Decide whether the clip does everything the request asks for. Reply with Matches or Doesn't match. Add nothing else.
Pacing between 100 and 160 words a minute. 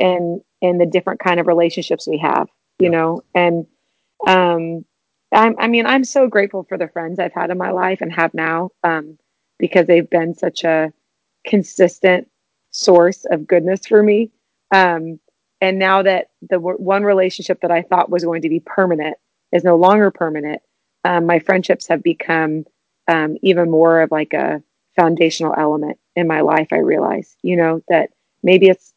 Doesn't match